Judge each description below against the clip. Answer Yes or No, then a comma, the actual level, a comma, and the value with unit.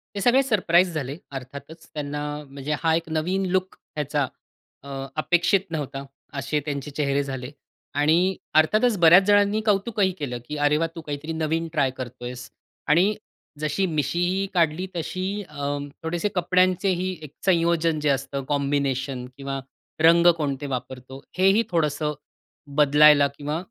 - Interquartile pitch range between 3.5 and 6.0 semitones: Yes, average, 4.0 semitones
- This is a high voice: No, medium, 155 Hz